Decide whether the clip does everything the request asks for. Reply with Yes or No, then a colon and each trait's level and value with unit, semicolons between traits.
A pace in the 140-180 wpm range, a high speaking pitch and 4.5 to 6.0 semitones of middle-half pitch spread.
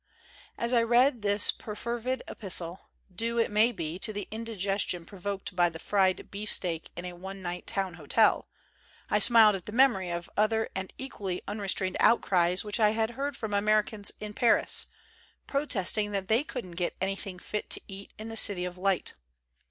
No: average, 175 wpm; high, 205 Hz; average, 3.3 semitones